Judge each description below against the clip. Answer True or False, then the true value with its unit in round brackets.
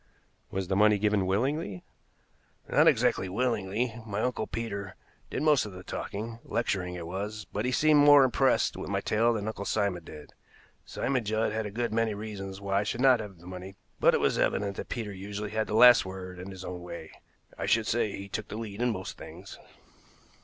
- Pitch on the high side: False (105 Hz)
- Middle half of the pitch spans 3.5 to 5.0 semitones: False (3.0 semitones)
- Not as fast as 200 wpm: False (205 wpm)